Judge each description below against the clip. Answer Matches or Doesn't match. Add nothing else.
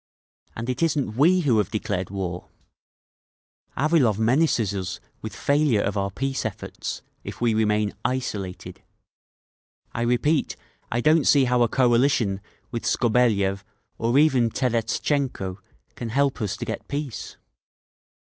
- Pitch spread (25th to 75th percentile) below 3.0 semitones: Doesn't match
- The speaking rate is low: Matches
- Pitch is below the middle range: Matches